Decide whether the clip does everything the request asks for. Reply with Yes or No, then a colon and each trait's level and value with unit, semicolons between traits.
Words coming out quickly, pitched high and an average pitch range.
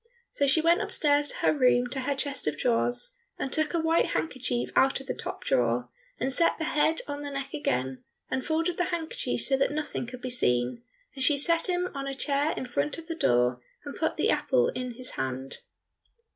Yes: fast, 215 wpm; very high, 275 Hz; average, 4.6 semitones